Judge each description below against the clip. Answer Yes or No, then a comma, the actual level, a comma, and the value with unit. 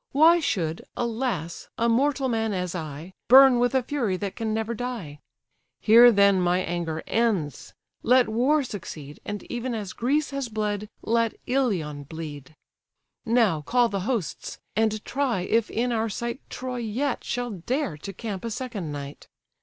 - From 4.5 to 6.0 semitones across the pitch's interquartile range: Yes, average, 5.2 semitones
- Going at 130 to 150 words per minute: No, average, 160 wpm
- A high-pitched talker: Yes, high, 225 Hz